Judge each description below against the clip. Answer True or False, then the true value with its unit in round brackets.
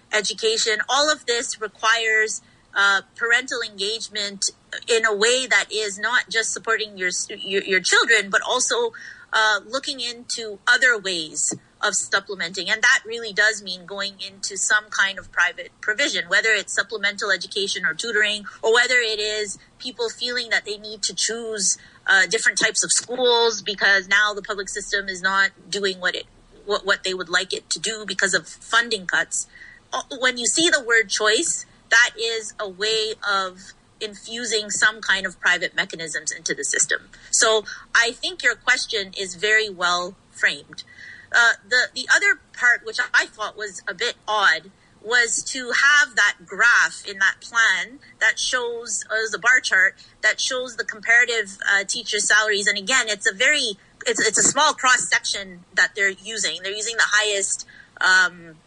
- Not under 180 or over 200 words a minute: False (170 wpm)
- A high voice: True (220 Hz)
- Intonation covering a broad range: False (3.5 semitones)